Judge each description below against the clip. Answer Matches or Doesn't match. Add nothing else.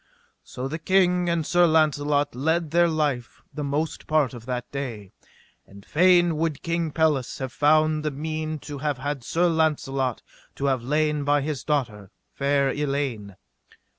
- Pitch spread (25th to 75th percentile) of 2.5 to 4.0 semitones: Matches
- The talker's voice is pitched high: Doesn't match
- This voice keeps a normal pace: Matches